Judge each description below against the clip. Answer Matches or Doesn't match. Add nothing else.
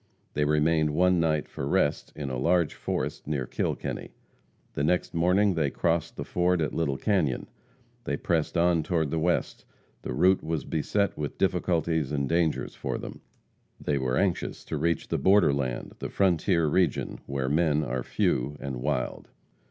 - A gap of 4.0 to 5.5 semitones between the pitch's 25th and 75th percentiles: Doesn't match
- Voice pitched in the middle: Doesn't match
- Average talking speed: Matches